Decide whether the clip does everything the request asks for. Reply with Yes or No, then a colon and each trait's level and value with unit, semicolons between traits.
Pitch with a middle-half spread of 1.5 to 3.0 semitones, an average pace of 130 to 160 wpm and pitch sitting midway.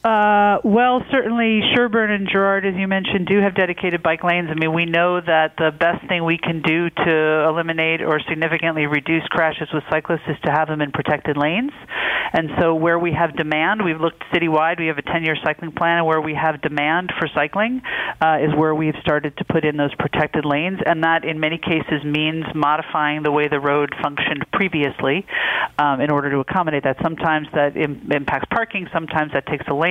No: narrow, 2.4 semitones; fast, 205 wpm; medium, 160 Hz